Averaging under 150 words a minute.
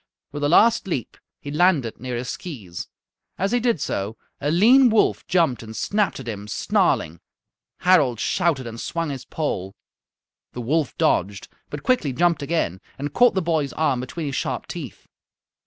No: average, 170 wpm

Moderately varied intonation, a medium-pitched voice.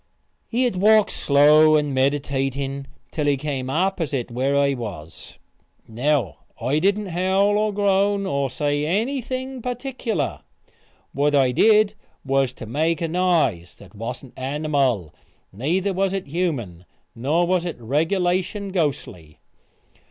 No: wide, 6.3 semitones; medium, 150 Hz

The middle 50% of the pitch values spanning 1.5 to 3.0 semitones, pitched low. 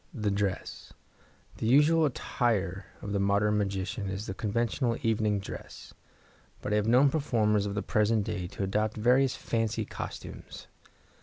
Yes: narrow, 2.6 semitones; low, 105 Hz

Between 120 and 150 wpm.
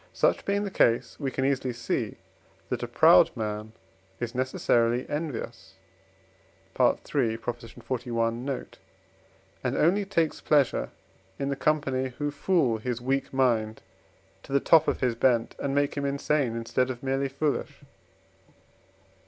Yes: slow, 135 wpm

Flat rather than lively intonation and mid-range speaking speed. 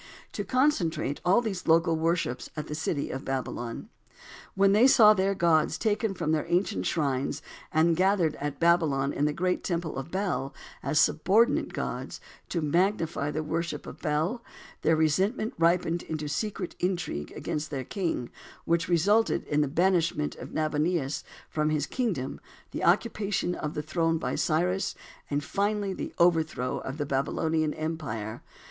No: average, 3.8 semitones; average, 155 wpm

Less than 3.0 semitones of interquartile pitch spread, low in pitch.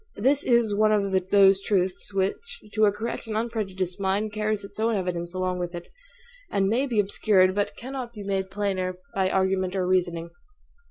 No: narrow, 2.5 semitones; high, 195 Hz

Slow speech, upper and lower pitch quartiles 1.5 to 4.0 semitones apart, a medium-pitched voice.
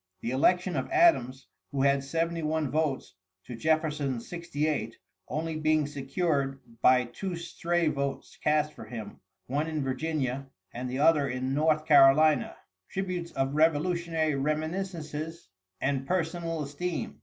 Yes: slow, 130 wpm; average, 3.3 semitones; medium, 155 Hz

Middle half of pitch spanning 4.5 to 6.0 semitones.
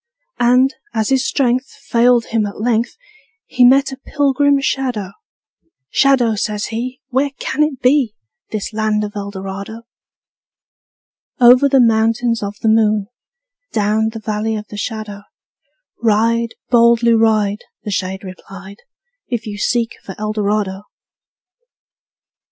No: average, 3.0 semitones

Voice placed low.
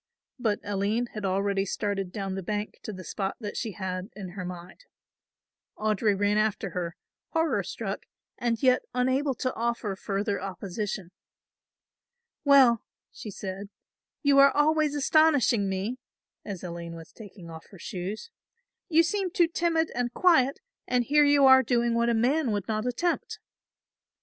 No: high, 215 Hz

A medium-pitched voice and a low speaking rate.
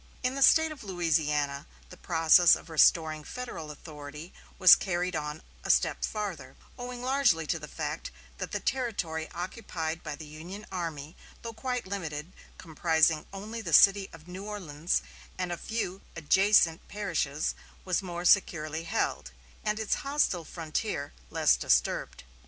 No: medium, 175 Hz; average, 145 wpm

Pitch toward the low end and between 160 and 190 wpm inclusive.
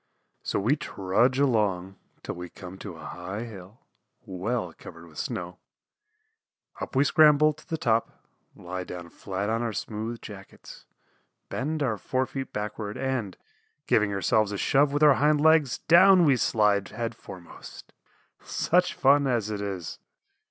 No: low, 110 Hz; average, 150 wpm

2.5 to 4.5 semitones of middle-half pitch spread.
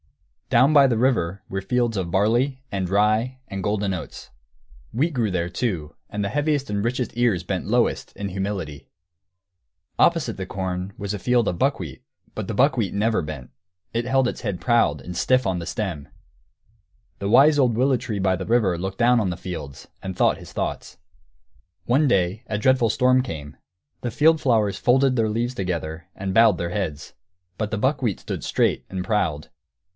No: average, 5.1 semitones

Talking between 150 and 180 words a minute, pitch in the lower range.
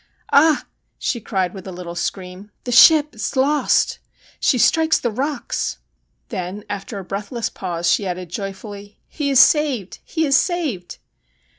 No: average, 165 wpm; high, 210 Hz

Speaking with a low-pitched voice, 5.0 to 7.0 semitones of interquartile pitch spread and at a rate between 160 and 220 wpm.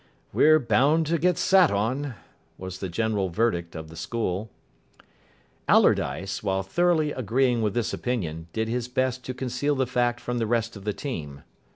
Yes: low, 120 Hz; average, 5.3 semitones; average, 170 wpm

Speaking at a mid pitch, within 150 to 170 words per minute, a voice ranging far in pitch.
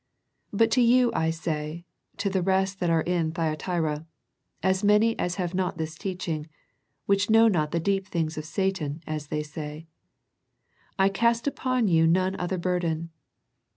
No: medium, 180 Hz; average, 160 wpm; average, 3.5 semitones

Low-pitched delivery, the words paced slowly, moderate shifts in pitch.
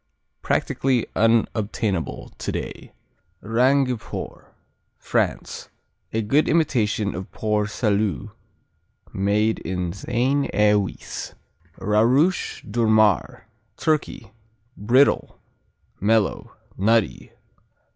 Yes: low, 110 Hz; slow, 75 wpm; average, 3.1 semitones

